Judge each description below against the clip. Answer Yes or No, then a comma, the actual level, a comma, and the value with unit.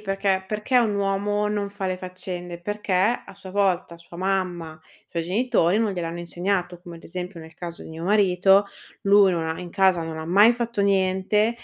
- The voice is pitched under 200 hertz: Yes, high, 190 Hz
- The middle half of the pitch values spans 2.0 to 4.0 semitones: Yes, average, 2.7 semitones